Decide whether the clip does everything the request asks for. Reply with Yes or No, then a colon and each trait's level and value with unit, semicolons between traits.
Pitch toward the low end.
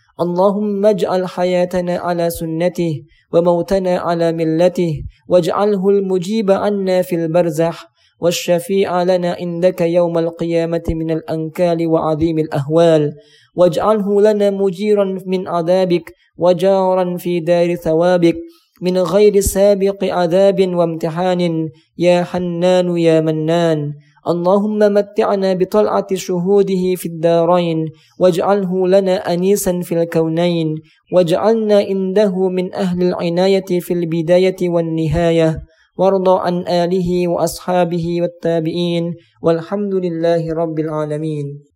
No: medium, 175 Hz